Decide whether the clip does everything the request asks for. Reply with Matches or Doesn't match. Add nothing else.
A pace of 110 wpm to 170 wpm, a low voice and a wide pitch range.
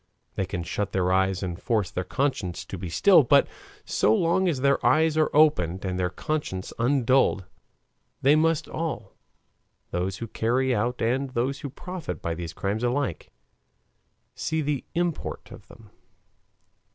Matches